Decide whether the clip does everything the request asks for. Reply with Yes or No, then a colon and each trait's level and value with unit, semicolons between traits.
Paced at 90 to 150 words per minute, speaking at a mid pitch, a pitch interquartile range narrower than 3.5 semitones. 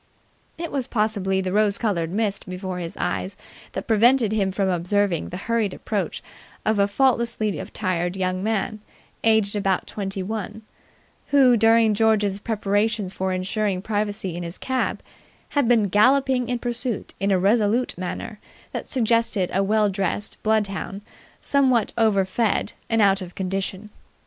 No: average, 145 wpm; high, 205 Hz; average, 2.9 semitones